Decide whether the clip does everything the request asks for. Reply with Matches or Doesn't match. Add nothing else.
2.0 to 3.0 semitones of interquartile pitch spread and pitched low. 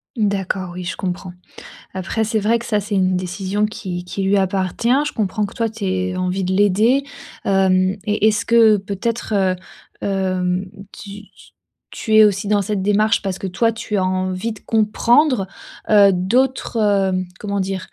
Doesn't match